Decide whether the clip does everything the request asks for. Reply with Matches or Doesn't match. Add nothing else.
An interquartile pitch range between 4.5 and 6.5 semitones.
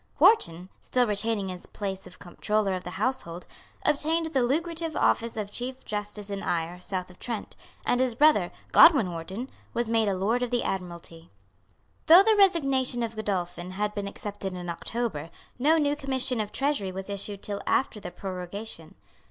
Matches